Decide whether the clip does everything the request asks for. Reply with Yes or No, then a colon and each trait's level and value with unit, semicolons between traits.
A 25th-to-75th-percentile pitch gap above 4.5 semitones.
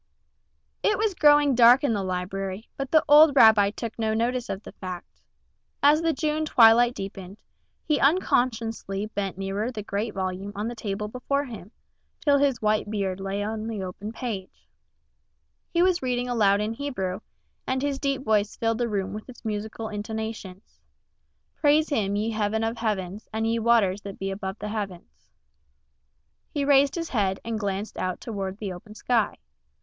No: average, 4.1 semitones